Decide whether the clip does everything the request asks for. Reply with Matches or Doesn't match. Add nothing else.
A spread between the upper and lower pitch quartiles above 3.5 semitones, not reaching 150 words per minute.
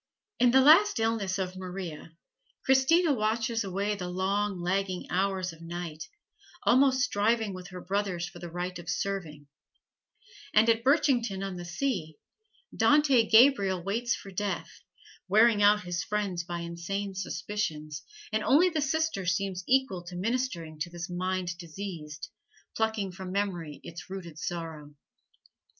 Matches